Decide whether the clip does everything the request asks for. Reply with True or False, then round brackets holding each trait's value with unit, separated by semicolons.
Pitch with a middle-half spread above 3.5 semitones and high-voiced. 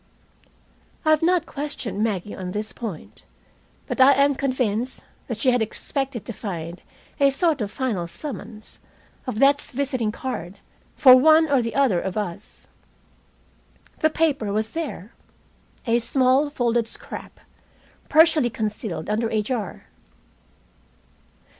True (4.8 semitones; 240 Hz)